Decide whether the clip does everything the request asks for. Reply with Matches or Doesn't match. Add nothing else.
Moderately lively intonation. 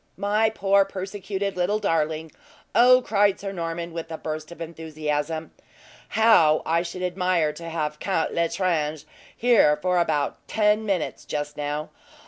Matches